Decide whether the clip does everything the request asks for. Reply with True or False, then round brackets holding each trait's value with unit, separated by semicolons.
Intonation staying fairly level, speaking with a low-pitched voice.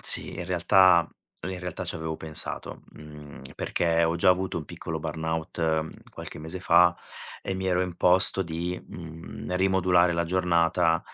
True (2.0 semitones; 85 Hz)